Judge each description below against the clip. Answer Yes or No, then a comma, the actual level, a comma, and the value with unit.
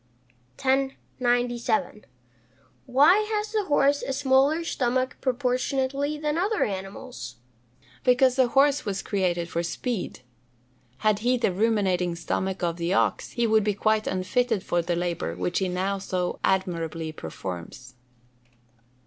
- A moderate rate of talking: No, slow, 130 wpm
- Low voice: No, high, 220 Hz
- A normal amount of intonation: No, wide, 6.6 semitones